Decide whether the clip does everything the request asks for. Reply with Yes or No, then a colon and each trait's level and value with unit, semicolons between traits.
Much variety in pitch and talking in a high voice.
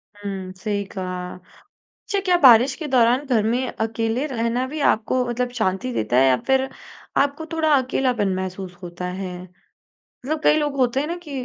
Yes: wide, 6.0 semitones; high, 240 Hz